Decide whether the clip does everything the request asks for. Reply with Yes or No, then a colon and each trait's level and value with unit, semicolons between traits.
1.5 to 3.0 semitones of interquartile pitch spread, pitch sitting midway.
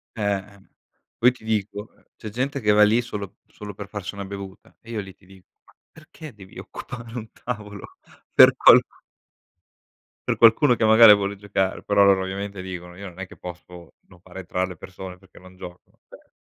No: narrow, 2.5 semitones; low, 100 Hz